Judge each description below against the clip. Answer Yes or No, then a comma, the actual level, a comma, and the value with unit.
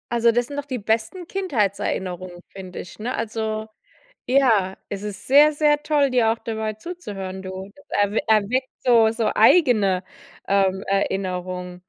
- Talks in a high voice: Yes, high, 220 Hz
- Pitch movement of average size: Yes, average, 4.7 semitones